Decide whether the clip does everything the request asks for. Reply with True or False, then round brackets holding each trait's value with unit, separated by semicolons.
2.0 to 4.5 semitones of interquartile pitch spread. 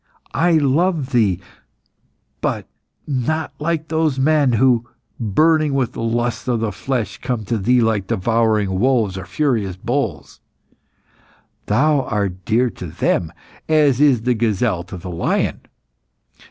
False (5.3 semitones)